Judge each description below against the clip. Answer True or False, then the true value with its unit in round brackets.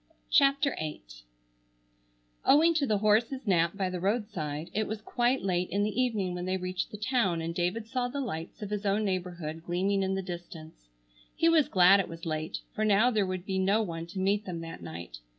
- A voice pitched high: True (195 Hz)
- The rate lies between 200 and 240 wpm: True (205 wpm)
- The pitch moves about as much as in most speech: True (3.9 semitones)